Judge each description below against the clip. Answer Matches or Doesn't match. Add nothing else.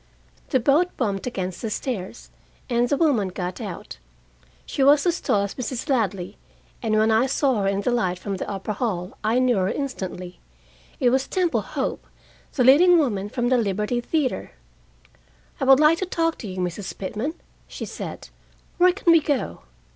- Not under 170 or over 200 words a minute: Matches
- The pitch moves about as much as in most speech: Doesn't match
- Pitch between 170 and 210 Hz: Doesn't match